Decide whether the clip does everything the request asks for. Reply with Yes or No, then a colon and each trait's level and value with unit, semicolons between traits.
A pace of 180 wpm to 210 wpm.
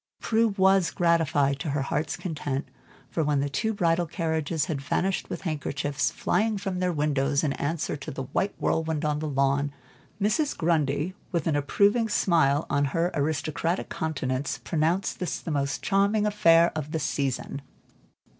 No: average, 160 wpm